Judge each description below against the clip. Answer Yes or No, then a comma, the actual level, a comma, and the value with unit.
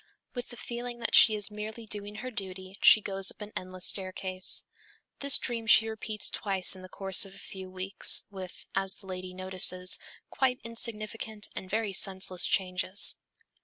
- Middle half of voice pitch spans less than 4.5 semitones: Yes, average, 2.8 semitones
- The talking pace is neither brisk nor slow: Yes, average, 170 wpm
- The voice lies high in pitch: Yes, high, 200 Hz